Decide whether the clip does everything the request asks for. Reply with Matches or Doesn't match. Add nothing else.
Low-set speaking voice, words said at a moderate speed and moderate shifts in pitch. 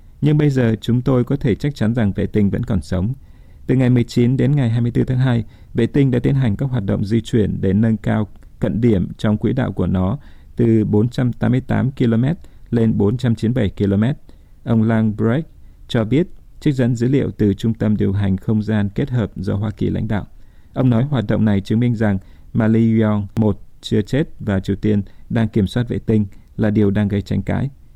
Matches